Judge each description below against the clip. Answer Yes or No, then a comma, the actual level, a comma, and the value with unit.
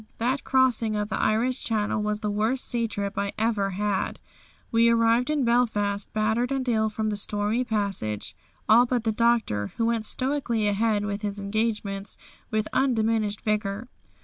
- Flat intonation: Yes, narrow, 2.2 semitones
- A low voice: No, high, 220 Hz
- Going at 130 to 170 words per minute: Yes, average, 165 wpm